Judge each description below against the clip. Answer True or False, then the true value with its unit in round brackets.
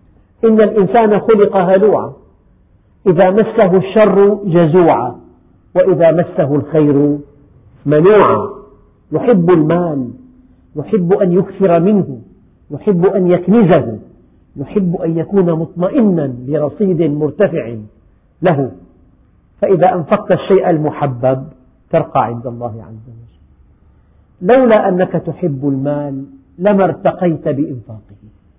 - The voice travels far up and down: True (6.5 semitones)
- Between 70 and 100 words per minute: True (90 wpm)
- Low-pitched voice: False (165 Hz)